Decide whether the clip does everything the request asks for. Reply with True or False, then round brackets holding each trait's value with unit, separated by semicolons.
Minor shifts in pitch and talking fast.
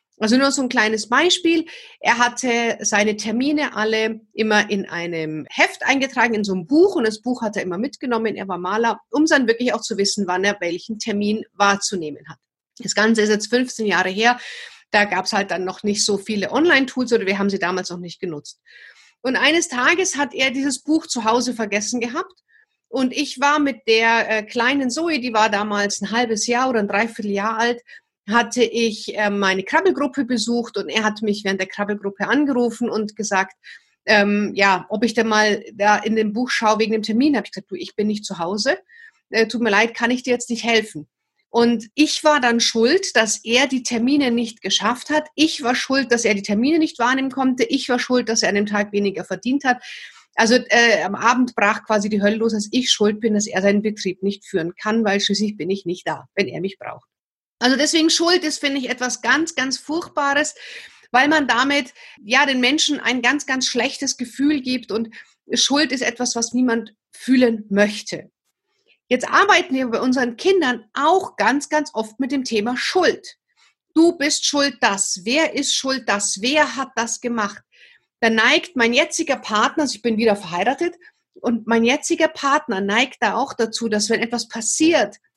False (4.7 semitones; 200 wpm)